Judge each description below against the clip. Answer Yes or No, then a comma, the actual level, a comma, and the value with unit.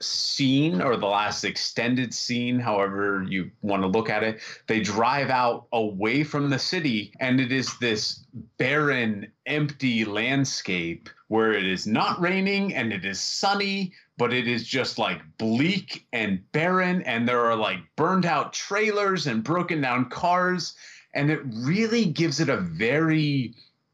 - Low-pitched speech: Yes, low, 130 Hz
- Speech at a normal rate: Yes, average, 155 wpm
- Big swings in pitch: Yes, wide, 6.5 semitones